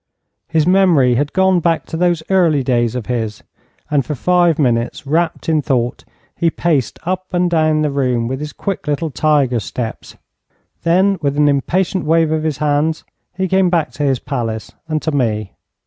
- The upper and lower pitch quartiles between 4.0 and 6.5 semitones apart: Yes, average, 4.4 semitones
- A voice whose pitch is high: No, medium, 155 Hz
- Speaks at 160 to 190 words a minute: Yes, average, 180 wpm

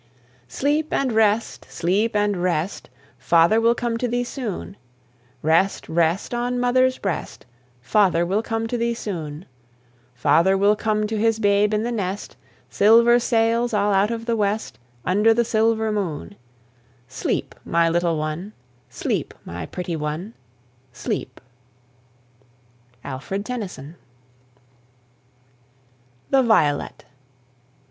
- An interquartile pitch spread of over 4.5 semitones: Yes, average, 4.9 semitones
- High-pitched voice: Yes, high, 210 Hz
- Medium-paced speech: No, slow, 120 wpm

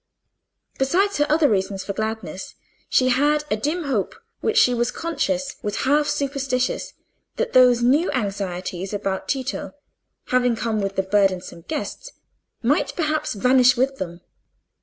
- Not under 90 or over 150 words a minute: Yes, average, 140 wpm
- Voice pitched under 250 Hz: No, very high, 255 Hz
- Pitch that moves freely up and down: Yes, wide, 6.2 semitones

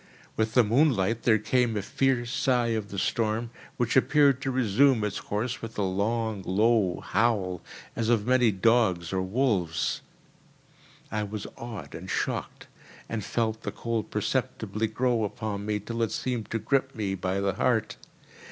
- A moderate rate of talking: Yes, average, 160 wpm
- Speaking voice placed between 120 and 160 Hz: No, low, 110 Hz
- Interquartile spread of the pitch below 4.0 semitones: Yes, average, 2.8 semitones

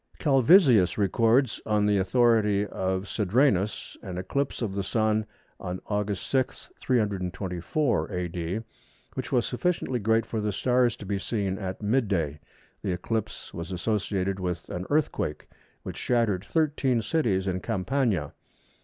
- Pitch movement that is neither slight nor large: Yes, average, 4.3 semitones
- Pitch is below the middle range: Yes, low, 105 Hz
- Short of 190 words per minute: Yes, slow, 135 wpm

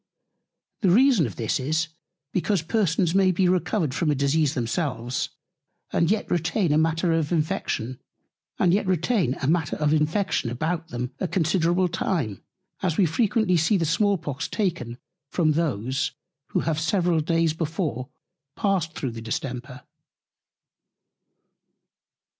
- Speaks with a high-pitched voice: No, medium, 165 Hz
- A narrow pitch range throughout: No, average, 4.2 semitones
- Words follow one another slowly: Yes, slow, 120 wpm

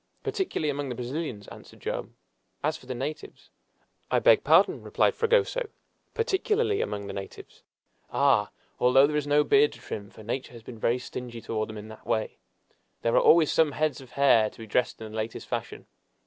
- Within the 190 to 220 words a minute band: Yes, average, 195 wpm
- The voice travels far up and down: Yes, wide, 5.8 semitones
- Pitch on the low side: Yes, low, 130 Hz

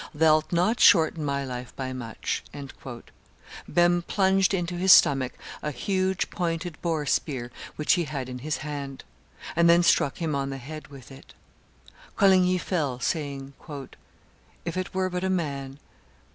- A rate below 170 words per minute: Yes, average, 150 wpm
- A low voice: No, medium, 155 Hz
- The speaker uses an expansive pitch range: No, average, 4.4 semitones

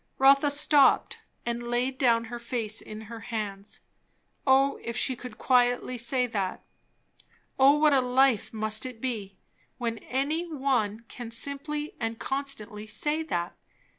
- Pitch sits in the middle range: No, high, 245 Hz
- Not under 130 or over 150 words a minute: Yes, average, 140 wpm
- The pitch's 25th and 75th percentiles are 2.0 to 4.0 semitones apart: Yes, average, 3.4 semitones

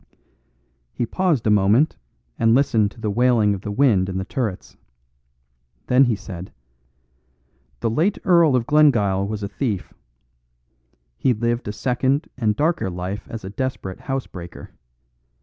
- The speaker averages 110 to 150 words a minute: Yes, average, 145 wpm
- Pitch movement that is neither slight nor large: Yes, average, 4.8 semitones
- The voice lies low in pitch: Yes, low, 115 Hz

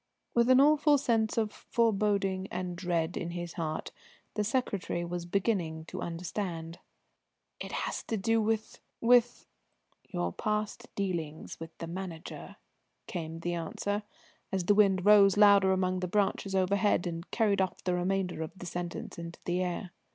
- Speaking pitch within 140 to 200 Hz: Yes, high, 190 Hz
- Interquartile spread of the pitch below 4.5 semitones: Yes, average, 3.4 semitones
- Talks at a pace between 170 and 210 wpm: No, average, 160 wpm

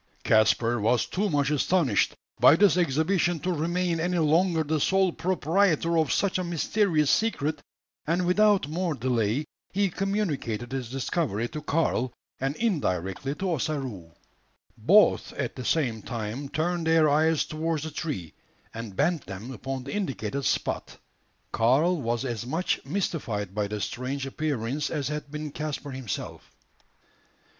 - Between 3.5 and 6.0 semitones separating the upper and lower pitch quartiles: Yes, wide, 5.5 semitones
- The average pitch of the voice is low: No, medium, 150 Hz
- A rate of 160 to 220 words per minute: No, average, 145 wpm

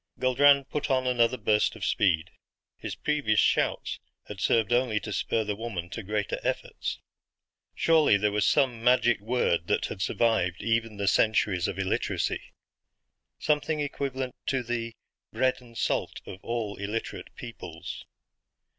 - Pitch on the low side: Yes, low, 115 Hz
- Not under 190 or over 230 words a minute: No, average, 145 wpm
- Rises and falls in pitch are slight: No, average, 3.9 semitones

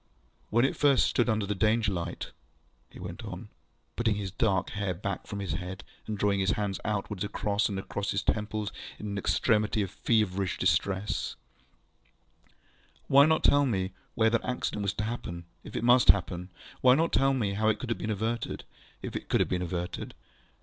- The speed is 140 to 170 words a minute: No, average, 180 wpm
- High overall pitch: No, low, 105 Hz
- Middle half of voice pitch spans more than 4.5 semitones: No, average, 2.9 semitones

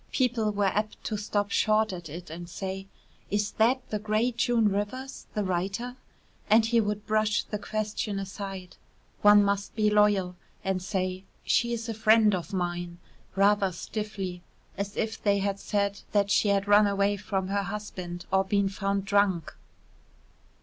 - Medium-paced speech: Yes, average, 165 wpm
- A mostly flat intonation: Yes, narrow, 1.8 semitones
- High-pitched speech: Yes, high, 205 Hz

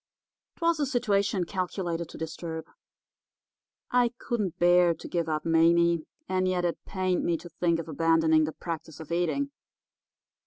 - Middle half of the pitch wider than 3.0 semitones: No, narrow, 2.4 semitones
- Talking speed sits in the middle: Yes, average, 150 wpm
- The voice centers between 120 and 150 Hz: No, medium, 170 Hz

